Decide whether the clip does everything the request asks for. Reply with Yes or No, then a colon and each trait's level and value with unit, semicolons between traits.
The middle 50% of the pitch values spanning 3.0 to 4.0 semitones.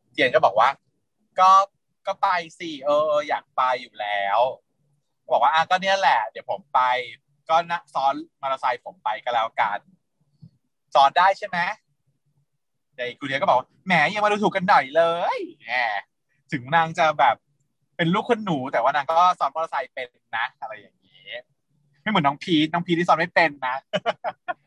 No: average, 4.5 semitones